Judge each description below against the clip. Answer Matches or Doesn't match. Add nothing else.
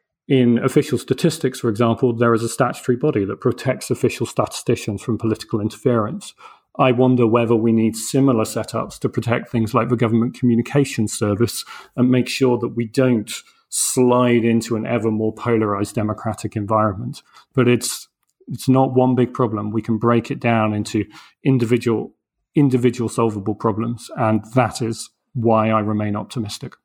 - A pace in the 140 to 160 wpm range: Matches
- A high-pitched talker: Doesn't match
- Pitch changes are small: Matches